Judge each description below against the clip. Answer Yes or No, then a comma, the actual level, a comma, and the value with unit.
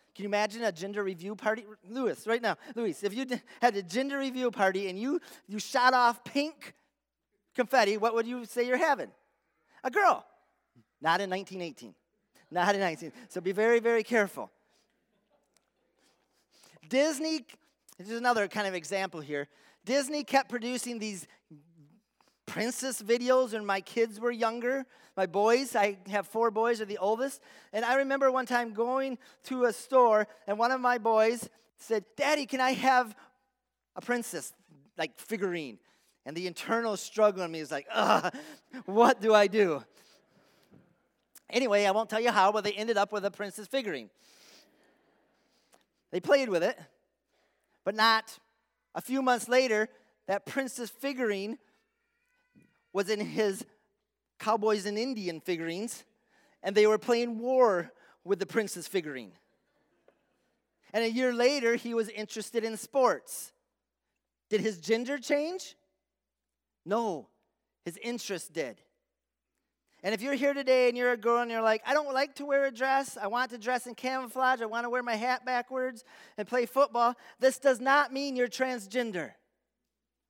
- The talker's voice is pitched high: Yes, high, 230 Hz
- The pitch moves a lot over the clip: No, average, 3.7 semitones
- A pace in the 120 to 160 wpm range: Yes, average, 155 wpm